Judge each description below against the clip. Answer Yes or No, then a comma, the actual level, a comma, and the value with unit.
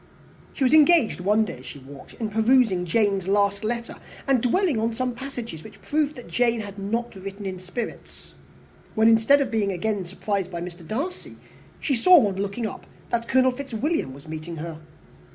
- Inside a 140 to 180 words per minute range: No, average, 190 wpm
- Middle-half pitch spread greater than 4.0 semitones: Yes, average, 4.7 semitones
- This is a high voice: Yes, high, 220 Hz